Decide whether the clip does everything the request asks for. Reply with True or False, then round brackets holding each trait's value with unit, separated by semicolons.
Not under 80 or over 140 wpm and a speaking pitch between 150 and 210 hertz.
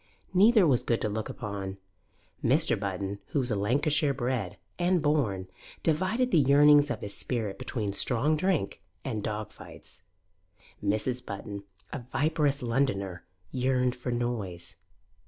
False (135 wpm; 125 Hz)